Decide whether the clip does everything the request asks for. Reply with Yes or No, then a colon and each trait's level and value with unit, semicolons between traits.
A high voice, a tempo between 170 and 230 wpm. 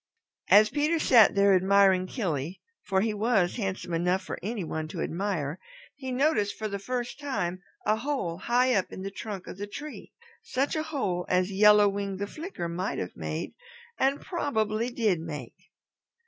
Yes: high, 200 Hz; average, 175 wpm